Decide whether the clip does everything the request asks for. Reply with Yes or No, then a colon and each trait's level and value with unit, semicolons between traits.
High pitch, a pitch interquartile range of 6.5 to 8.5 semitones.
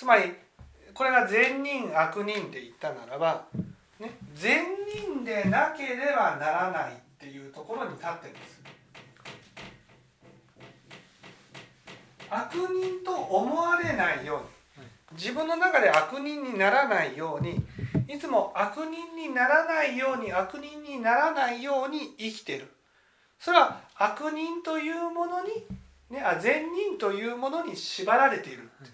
Yes: very high, 275 Hz; wide, 7.8 semitones